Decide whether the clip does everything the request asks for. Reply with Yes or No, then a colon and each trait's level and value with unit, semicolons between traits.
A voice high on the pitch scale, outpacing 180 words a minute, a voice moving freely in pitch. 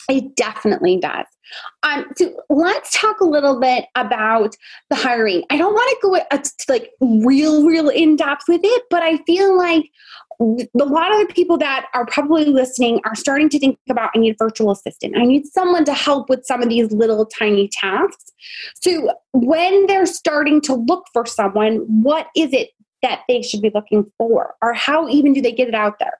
Yes: very high, 280 Hz; average, 195 wpm; wide, 6.4 semitones